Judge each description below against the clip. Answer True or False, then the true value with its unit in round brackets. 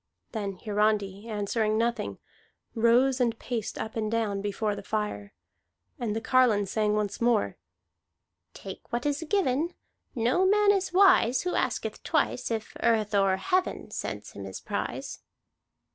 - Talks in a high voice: True (225 Hz)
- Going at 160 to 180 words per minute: False (145 wpm)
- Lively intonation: False (3.4 semitones)